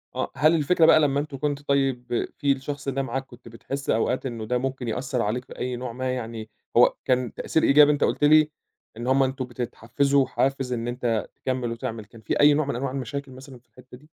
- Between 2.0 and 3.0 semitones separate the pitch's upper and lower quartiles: Yes, narrow, 2.4 semitones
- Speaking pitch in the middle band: No, low, 130 Hz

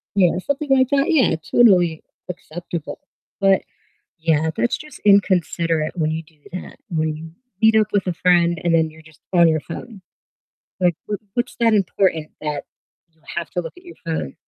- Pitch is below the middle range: No, medium, 175 Hz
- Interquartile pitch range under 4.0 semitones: No, average, 4.3 semitones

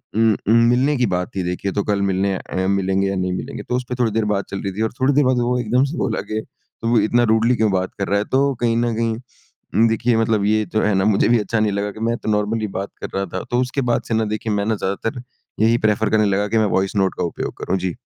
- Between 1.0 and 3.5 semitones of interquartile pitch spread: Yes, average, 2.9 semitones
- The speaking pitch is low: Yes, low, 110 Hz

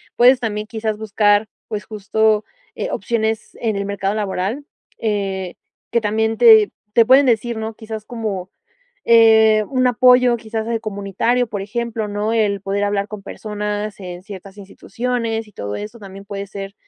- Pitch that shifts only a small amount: Yes, narrow, 2.0 semitones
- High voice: Yes, high, 215 Hz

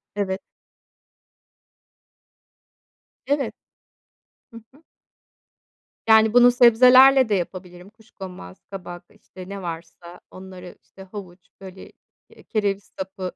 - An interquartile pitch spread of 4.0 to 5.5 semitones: No, average, 3.5 semitones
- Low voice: No, high, 195 Hz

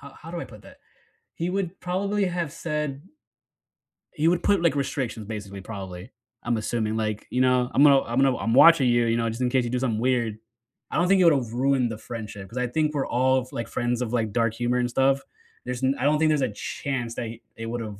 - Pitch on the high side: No, low, 125 Hz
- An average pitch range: Yes, average, 4.2 semitones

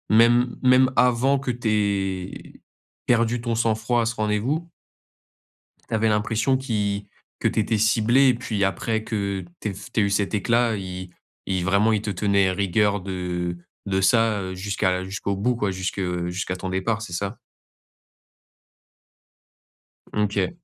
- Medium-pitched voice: No, low, 105 Hz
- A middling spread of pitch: Yes, average, 3.2 semitones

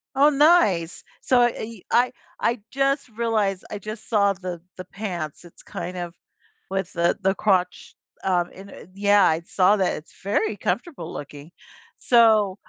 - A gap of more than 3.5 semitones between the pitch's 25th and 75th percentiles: Yes, average, 4.4 semitones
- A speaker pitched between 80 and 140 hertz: No, high, 200 Hz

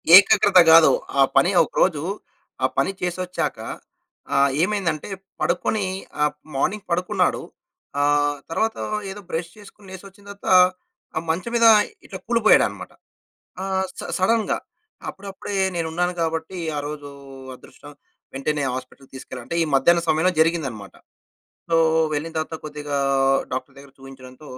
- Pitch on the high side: No, medium, 165 Hz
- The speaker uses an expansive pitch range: No, average, 4.6 semitones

